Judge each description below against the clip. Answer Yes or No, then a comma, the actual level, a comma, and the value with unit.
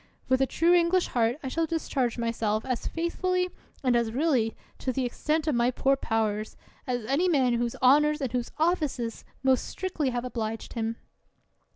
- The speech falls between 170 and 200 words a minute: Yes, average, 175 wpm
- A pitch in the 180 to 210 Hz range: No, very high, 255 Hz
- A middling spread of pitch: Yes, average, 4.8 semitones